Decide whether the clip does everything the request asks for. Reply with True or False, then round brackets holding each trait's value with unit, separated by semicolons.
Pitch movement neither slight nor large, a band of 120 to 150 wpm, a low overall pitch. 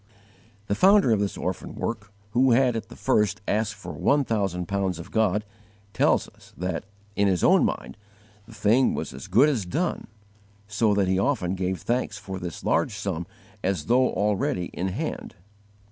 False (3.8 semitones; 175 wpm; 100 Hz)